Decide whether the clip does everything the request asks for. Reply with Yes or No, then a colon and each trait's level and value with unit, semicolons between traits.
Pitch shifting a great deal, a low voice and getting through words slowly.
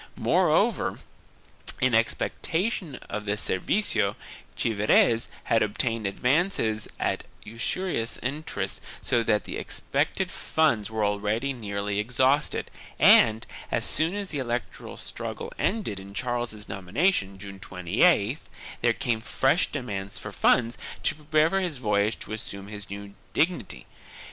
Yes: wide, 5.7 semitones; low, 115 Hz; slow, 125 wpm